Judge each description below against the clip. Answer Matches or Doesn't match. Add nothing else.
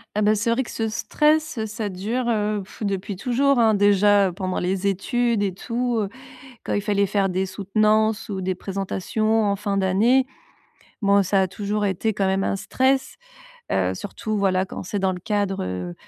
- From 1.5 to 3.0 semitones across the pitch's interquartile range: Matches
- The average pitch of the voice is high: Matches